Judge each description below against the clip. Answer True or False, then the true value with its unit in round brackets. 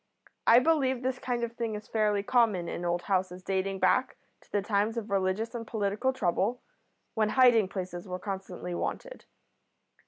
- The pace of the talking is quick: False (165 wpm)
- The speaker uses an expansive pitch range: False (4.1 semitones)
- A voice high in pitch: True (210 Hz)